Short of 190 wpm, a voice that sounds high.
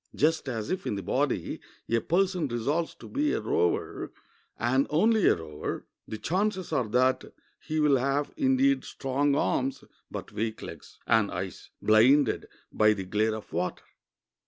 No: average, 160 wpm; low, 135 Hz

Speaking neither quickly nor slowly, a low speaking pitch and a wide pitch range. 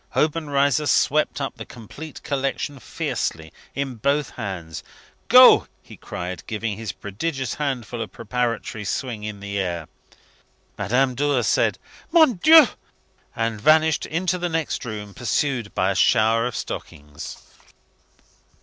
No: slow, 130 wpm; low, 125 Hz; wide, 5.8 semitones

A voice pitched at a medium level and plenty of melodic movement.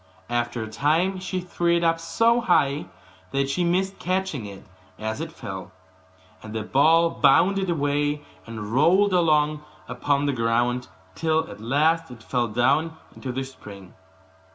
Yes: medium, 145 Hz; wide, 5.7 semitones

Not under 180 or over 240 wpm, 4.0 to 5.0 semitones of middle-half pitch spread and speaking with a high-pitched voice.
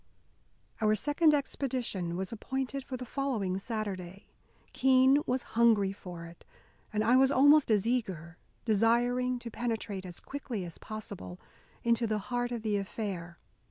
No: average, 145 wpm; average, 4.6 semitones; high, 225 Hz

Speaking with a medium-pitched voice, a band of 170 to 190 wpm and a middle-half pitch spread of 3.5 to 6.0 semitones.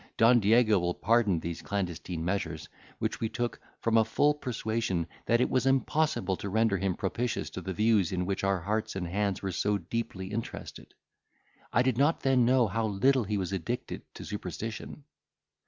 No: low, 105 Hz; average, 180 wpm; average, 3.8 semitones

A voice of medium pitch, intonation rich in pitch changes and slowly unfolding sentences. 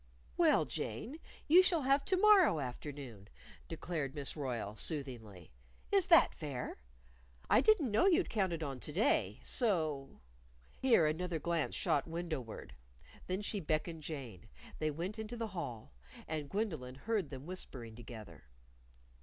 No: medium, 155 Hz; wide, 8.8 semitones; average, 145 wpm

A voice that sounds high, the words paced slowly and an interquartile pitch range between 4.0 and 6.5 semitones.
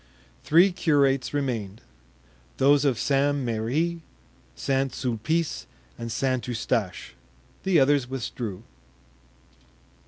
No: low, 130 Hz; slow, 85 wpm; average, 4.4 semitones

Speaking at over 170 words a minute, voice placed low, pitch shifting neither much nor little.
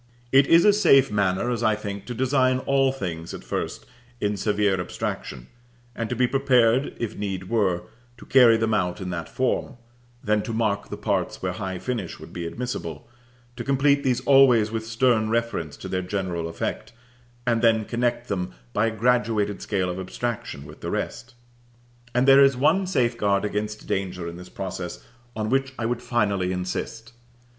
Yes: average, 180 wpm; low, 110 Hz; average, 4.6 semitones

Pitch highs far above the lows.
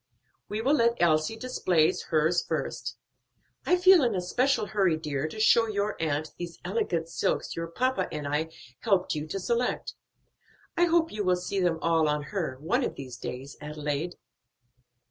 Yes: wide, 6.3 semitones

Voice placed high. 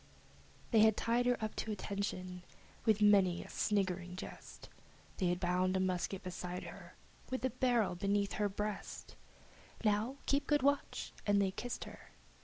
Yes: high, 205 Hz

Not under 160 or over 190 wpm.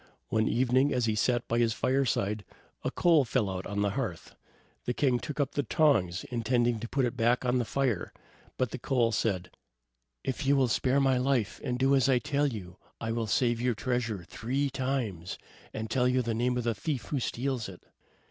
No: fast, 205 wpm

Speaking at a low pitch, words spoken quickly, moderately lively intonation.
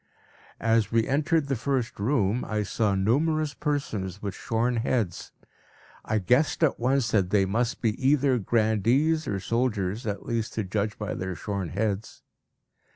No: low, 115 Hz; average, 155 wpm; average, 4.3 semitones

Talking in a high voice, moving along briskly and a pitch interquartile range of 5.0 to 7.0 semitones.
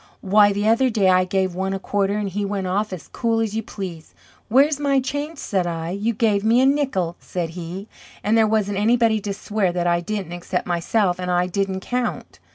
No: high, 200 Hz; fast, 215 wpm; average, 3.5 semitones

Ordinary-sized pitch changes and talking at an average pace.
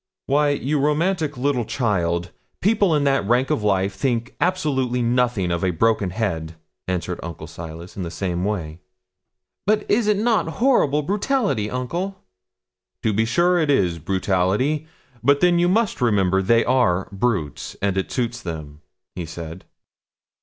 No: wide, 8.5 semitones; average, 155 wpm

